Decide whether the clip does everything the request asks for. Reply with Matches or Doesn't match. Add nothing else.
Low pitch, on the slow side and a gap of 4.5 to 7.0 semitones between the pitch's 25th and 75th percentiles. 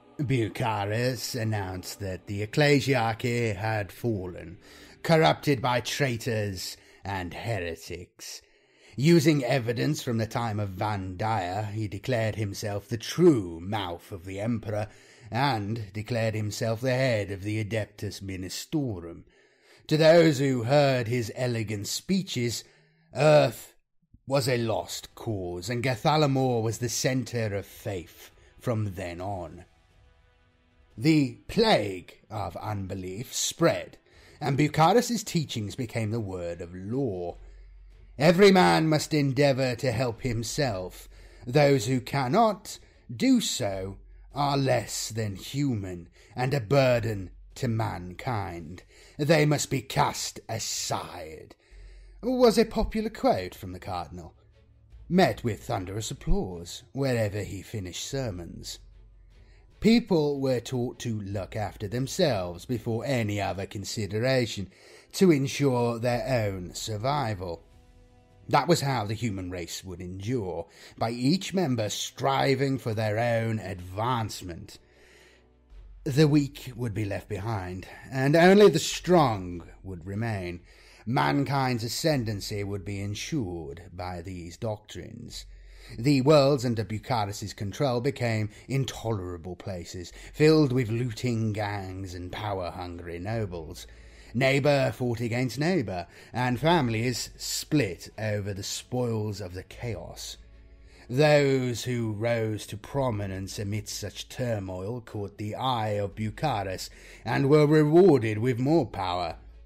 Matches